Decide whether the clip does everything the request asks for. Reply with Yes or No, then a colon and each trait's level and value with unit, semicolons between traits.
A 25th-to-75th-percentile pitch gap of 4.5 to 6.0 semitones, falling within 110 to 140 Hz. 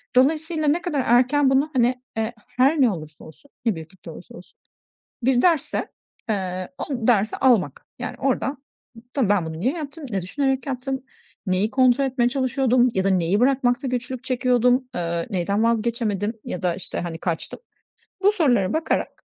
No: wide, 5.4 semitones; high, 245 Hz